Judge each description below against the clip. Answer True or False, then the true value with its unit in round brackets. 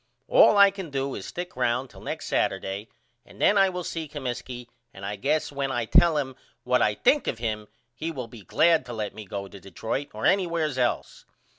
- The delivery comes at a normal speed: False (210 wpm)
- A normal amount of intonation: False (6.8 semitones)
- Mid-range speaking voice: False (130 Hz)